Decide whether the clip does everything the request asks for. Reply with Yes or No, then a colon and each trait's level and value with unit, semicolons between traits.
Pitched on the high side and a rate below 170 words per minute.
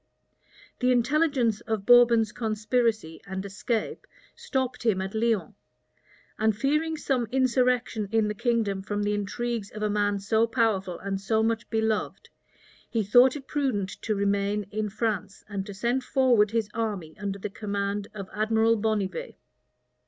Yes: high, 220 Hz; average, 150 wpm